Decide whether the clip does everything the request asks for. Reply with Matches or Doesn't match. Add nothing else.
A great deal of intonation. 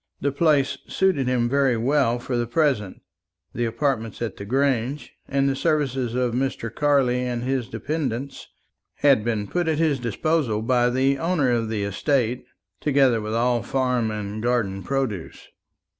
Doesn't match